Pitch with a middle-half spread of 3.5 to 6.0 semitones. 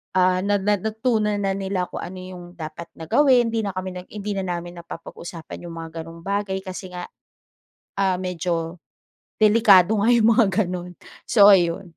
No: average, 2.9 semitones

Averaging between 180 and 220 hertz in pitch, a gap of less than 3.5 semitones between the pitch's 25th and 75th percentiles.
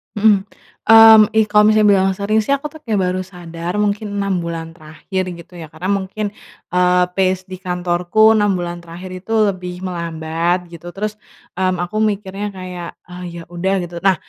Yes: medium, 185 Hz; average, 2.9 semitones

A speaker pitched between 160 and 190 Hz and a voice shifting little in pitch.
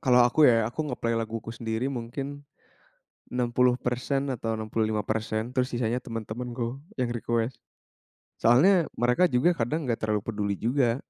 No: low, 120 Hz; narrow, 1.8 semitones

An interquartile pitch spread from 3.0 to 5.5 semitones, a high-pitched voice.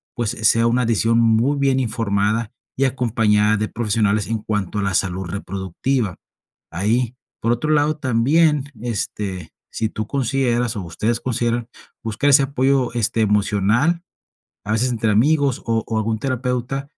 No: average, 3.4 semitones; low, 115 Hz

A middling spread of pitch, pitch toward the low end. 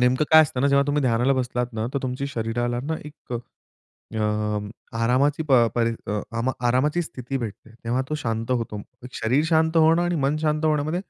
Yes: average, 4.3 semitones; low, 130 Hz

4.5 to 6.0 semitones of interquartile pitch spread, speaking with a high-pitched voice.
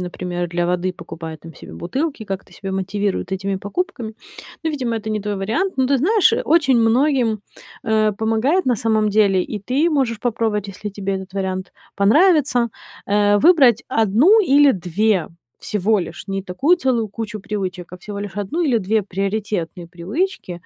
Yes: average, 4.9 semitones; high, 210 Hz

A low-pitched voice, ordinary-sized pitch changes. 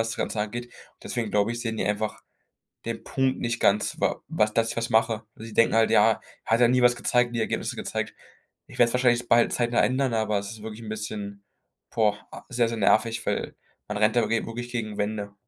No: low, 115 Hz; narrow, 1.9 semitones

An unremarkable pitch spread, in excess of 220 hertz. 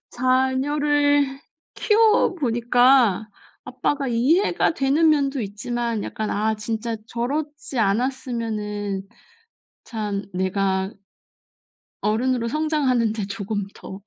Yes: average, 4.6 semitones; high, 240 Hz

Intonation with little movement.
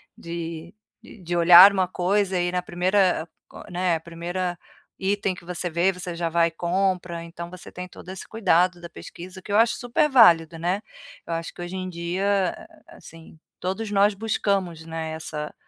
Yes: narrow, 2.1 semitones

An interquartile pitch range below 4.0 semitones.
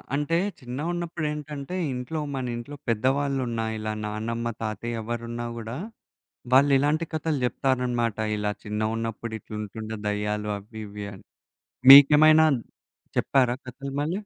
No: average, 4.6 semitones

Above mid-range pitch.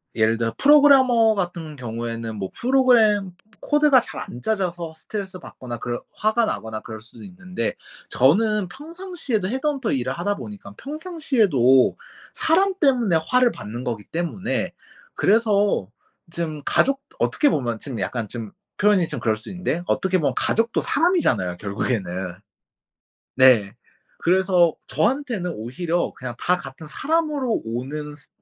No: medium, 180 Hz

